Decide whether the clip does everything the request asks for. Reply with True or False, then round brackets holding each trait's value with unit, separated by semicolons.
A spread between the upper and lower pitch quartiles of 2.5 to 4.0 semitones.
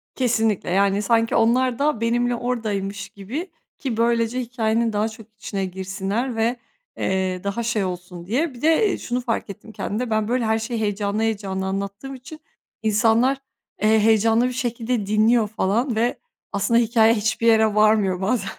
True (2.8 semitones)